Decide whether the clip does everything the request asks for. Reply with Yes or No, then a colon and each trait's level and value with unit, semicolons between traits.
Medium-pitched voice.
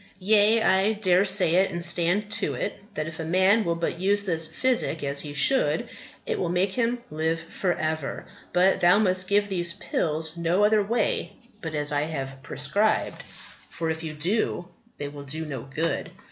Yes: medium, 175 Hz